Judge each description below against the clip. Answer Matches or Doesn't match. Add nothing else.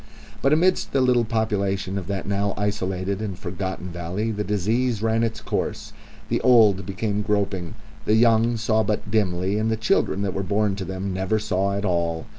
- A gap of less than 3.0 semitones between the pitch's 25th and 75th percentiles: Matches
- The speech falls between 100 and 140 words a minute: Doesn't match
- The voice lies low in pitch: Matches